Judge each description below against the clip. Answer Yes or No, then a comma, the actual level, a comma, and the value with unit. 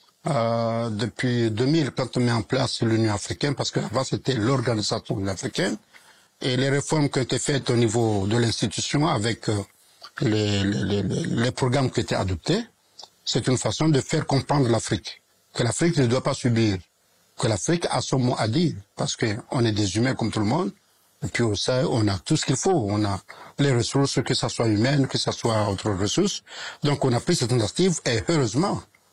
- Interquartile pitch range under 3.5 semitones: No, average, 3.8 semitones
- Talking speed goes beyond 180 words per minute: Yes, average, 200 wpm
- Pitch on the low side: Yes, low, 120 Hz